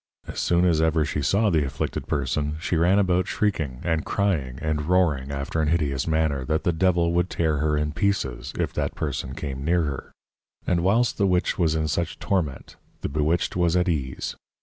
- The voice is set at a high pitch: No, very low, 80 Hz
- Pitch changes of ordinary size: Yes, average, 3.3 semitones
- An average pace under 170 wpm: No, average, 195 wpm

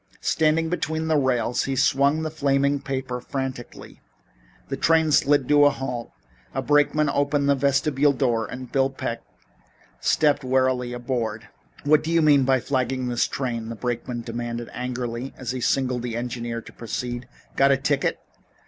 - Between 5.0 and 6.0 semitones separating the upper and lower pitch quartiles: No, average, 2.8 semitones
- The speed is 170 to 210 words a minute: No, average, 160 wpm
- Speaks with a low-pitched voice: Yes, low, 130 Hz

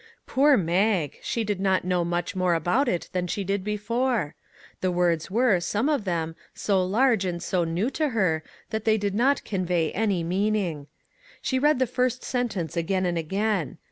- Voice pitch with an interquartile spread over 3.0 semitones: Yes, average, 4.4 semitones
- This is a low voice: No, high, 195 Hz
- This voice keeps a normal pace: Yes, average, 180 wpm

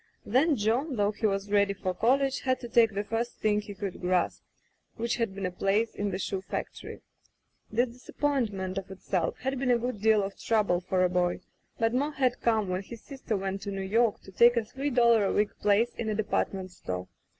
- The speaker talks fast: Yes, fast, 215 wpm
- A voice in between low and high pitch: No, high, 215 Hz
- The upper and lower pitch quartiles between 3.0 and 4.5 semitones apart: Yes, average, 3.5 semitones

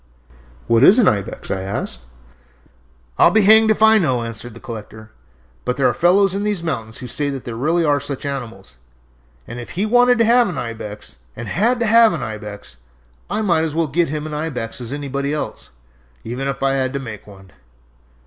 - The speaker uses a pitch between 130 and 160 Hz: Yes, medium, 140 Hz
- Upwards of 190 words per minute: Yes, fast, 205 wpm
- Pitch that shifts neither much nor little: No, wide, 8.0 semitones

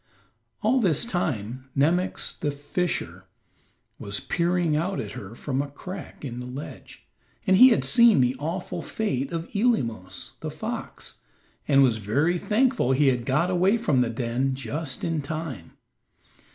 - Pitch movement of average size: No, wide, 6.0 semitones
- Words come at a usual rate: Yes, average, 150 wpm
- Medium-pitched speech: Yes, medium, 145 Hz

